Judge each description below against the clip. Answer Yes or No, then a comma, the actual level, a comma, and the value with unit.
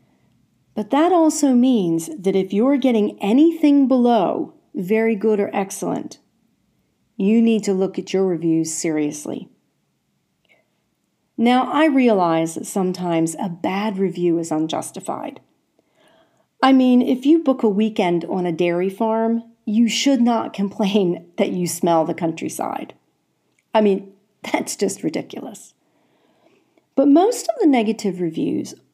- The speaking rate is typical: No, slow, 130 wpm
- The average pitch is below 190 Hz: No, high, 210 Hz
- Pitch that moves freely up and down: Yes, wide, 5.9 semitones